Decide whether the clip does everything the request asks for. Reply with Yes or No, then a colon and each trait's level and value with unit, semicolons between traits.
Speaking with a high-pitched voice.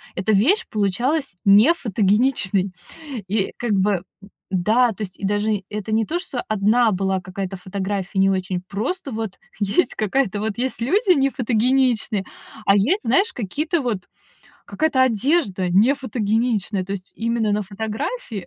Yes: high, 215 Hz